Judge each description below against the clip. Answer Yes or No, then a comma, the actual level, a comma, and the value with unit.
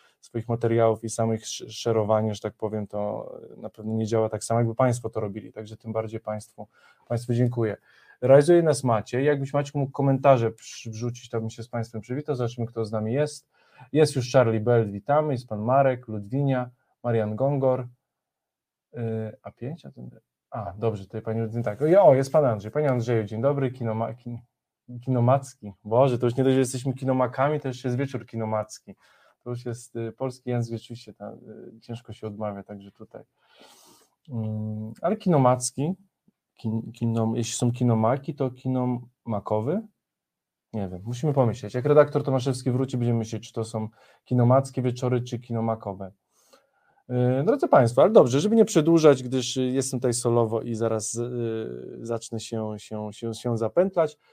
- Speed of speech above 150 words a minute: Yes, fast, 160 wpm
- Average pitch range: Yes, average, 3.0 semitones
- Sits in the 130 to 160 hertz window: No, low, 120 Hz